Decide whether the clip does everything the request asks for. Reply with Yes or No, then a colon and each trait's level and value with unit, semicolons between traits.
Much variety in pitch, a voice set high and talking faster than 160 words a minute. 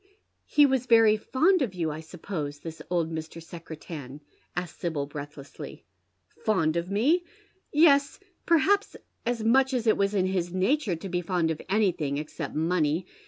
No: wide, 6.4 semitones; medium, 180 Hz; average, 175 wpm